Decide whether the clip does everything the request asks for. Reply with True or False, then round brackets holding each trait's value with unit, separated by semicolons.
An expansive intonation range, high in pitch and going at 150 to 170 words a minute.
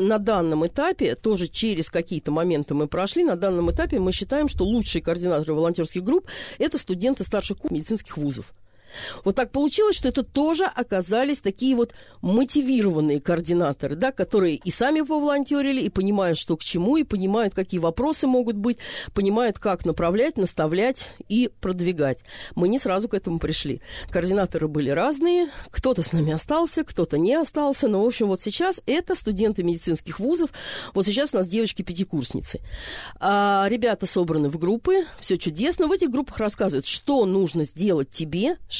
True (7.4 semitones; 200 Hz; 160 wpm)